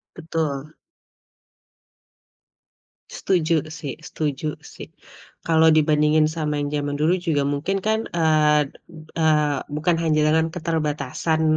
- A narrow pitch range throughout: Yes, narrow, 1.4 semitones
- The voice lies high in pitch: No, medium, 155 Hz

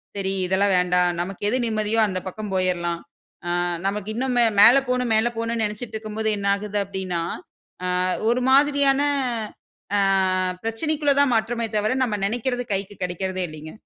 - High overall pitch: Yes, high, 215 Hz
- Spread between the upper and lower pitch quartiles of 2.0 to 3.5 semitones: No, average, 4.2 semitones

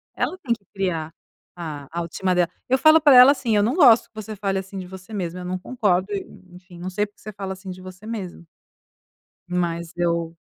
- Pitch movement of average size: Yes, average, 3.4 semitones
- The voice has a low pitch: No, high, 190 Hz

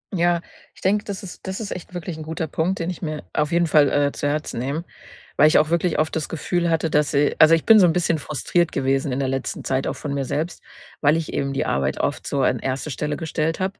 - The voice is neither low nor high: Yes, medium, 155 Hz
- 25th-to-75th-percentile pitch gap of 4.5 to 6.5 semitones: No, average, 3.1 semitones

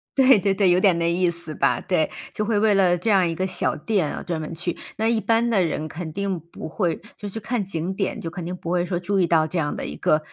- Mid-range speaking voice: Yes, medium, 180 Hz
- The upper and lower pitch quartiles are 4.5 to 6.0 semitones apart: No, average, 3.3 semitones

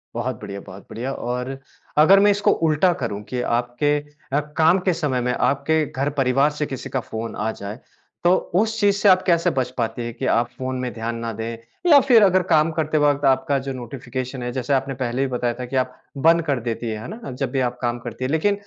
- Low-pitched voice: Yes, low, 130 Hz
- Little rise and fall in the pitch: No, average, 4.4 semitones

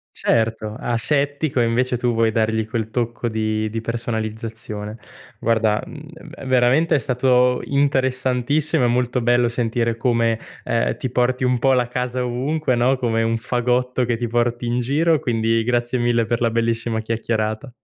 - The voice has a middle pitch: No, low, 120 Hz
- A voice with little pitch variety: Yes, narrow, 1.8 semitones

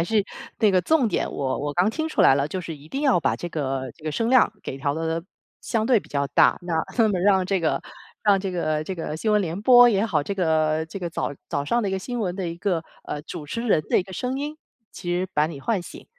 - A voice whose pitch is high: No, medium, 180 Hz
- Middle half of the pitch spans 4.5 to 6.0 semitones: Yes, wide, 5.5 semitones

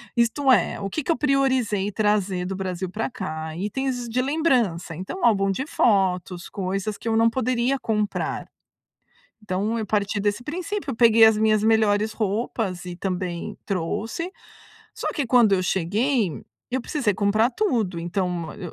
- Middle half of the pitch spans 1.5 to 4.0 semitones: No, average, 4.4 semitones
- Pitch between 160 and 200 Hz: No, high, 215 Hz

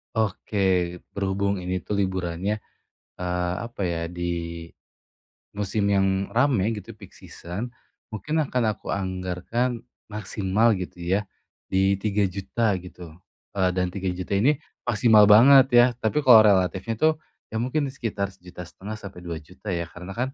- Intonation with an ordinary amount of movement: Yes, average, 3.4 semitones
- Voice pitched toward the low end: Yes, low, 100 Hz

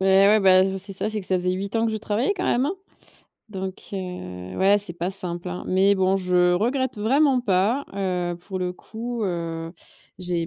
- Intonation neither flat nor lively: Yes, average, 3.1 semitones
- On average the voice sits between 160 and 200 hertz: Yes, high, 190 Hz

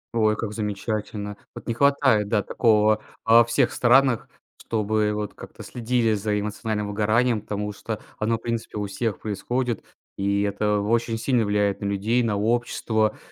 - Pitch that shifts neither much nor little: No, narrow, 2.0 semitones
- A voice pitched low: Yes, low, 110 Hz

